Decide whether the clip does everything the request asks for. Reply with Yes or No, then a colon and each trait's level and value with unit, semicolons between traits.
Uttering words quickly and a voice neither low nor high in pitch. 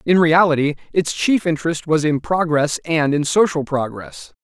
No: average, 160 wpm; medium, 160 Hz